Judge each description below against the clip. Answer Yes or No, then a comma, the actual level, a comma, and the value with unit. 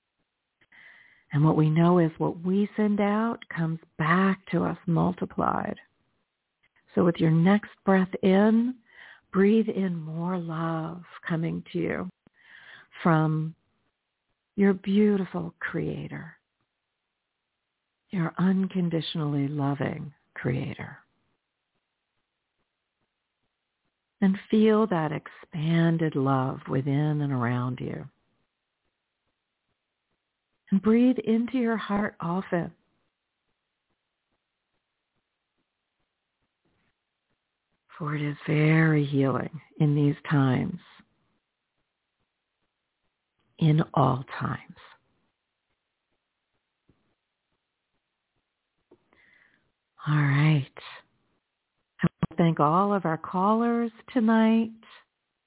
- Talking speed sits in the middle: No, slow, 80 wpm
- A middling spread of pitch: Yes, average, 4.8 semitones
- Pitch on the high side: No, medium, 165 Hz